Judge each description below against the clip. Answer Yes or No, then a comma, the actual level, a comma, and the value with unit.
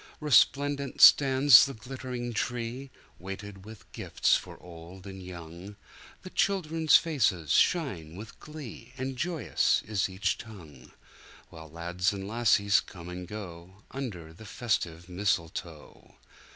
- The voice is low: Yes, low, 105 Hz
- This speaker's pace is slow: Yes, slow, 110 wpm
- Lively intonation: Yes, wide, 6.7 semitones